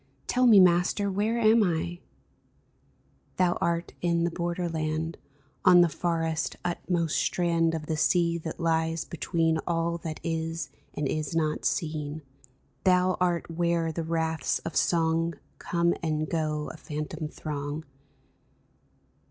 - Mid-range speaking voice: Yes, medium, 165 Hz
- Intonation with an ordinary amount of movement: No, narrow, 1.5 semitones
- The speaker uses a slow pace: No, average, 145 wpm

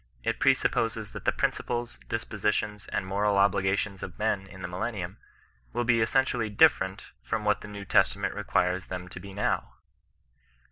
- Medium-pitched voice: No, low, 100 Hz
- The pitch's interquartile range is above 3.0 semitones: No, average, 2.7 semitones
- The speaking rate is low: No, average, 155 wpm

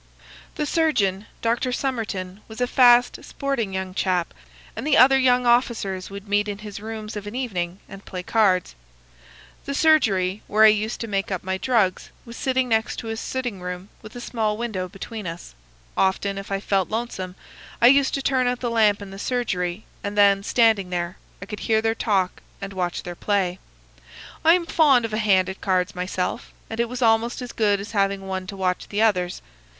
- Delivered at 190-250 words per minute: Yes, average, 195 wpm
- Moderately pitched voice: No, high, 210 Hz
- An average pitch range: Yes, average, 4.0 semitones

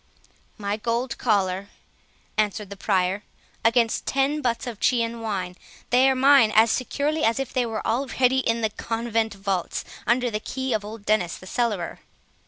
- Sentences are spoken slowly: No, average, 160 wpm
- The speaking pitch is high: Yes, high, 230 Hz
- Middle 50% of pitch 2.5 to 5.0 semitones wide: Yes, average, 3.4 semitones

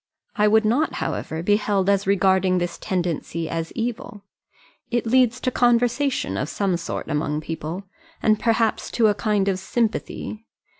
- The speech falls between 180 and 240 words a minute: No, average, 155 wpm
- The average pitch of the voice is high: Yes, high, 205 Hz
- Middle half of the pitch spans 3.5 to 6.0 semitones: Yes, average, 4.6 semitones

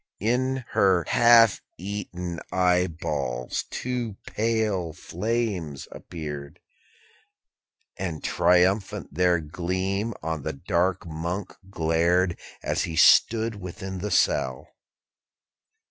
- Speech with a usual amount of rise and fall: Yes, average, 3.9 semitones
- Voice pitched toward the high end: No, very low, 90 Hz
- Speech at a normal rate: No, slow, 90 wpm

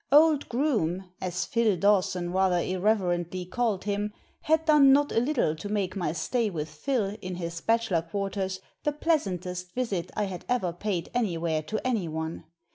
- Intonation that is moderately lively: Yes, average, 4.9 semitones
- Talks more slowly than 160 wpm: No, average, 170 wpm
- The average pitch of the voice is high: Yes, high, 195 Hz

